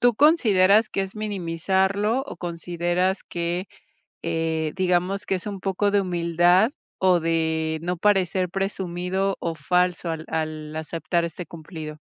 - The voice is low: No, medium, 180 Hz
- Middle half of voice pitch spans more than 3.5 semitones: No, narrow, 2.6 semitones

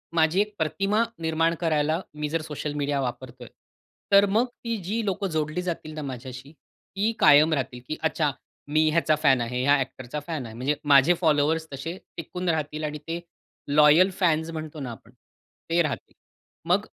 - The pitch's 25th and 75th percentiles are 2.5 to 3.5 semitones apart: Yes, average, 2.8 semitones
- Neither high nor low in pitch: Yes, medium, 155 Hz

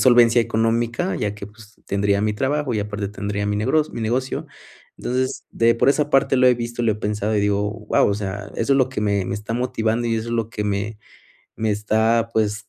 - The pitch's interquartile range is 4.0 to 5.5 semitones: No, narrow, 2.4 semitones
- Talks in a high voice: No, low, 110 Hz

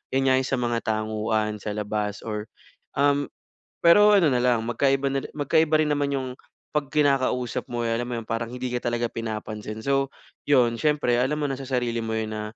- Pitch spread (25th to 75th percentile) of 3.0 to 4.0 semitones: Yes, average, 3.7 semitones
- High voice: No, low, 125 Hz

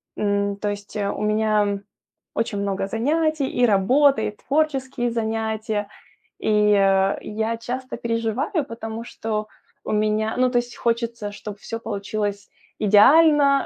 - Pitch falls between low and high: No, high, 220 Hz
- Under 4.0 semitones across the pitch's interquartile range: Yes, average, 2.9 semitones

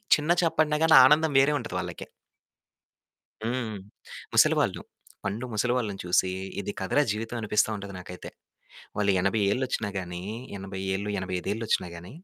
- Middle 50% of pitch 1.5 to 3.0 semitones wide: No, average, 4.7 semitones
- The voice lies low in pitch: Yes, low, 105 Hz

